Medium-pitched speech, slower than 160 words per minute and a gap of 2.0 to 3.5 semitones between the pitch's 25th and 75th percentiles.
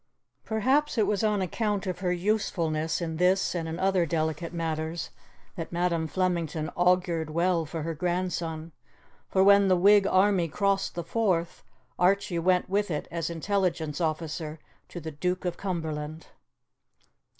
Yes: medium, 175 Hz; average, 150 wpm; average, 2.9 semitones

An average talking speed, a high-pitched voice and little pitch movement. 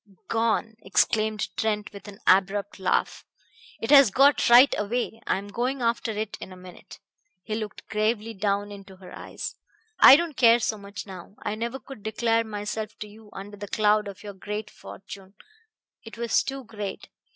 Yes: average, 175 wpm; high, 215 Hz; narrow, 2.2 semitones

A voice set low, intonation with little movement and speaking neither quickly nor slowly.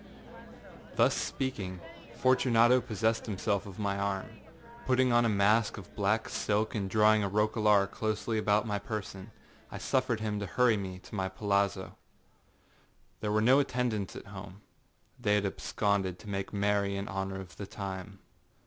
Yes: low, 105 Hz; narrow, 2.0 semitones; average, 160 wpm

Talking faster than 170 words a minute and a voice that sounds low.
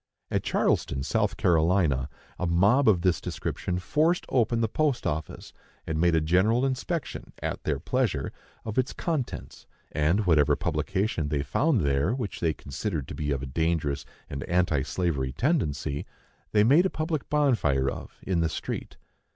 No: average, 160 wpm; very low, 90 Hz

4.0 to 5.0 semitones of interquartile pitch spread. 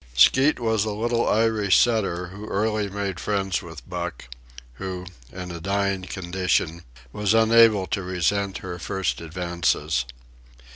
No: average, 3.2 semitones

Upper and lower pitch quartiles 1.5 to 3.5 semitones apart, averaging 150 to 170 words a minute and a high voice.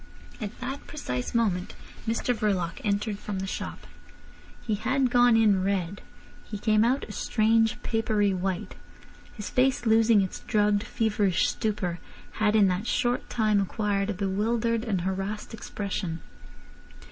No: narrow, 2.6 semitones; average, 140 wpm; high, 210 Hz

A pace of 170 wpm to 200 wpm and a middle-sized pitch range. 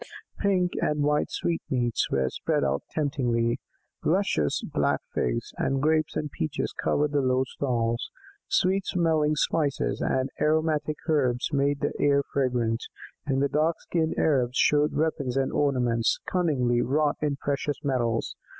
No: slow, 135 wpm; average, 3.6 semitones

